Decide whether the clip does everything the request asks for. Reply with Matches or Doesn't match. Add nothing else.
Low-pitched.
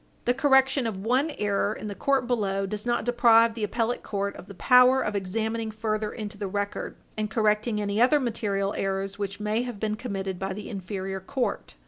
Doesn't match